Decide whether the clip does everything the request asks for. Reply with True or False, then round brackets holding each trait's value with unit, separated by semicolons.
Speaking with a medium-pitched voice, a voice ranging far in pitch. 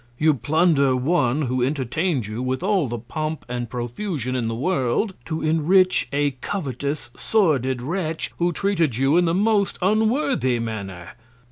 True (145 Hz; 6.1 semitones)